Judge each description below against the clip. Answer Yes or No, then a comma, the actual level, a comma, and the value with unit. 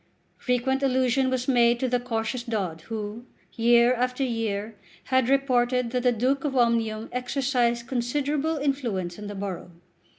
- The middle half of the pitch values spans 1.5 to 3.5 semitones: Yes, narrow, 2.4 semitones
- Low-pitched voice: No, high, 245 Hz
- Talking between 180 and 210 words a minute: No, average, 145 wpm